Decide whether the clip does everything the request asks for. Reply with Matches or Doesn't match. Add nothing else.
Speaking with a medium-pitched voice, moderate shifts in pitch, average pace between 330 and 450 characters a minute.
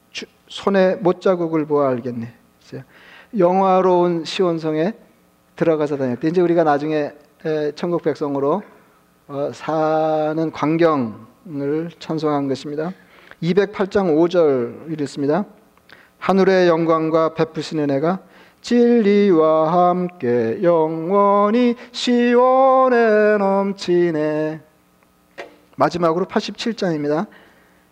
Doesn't match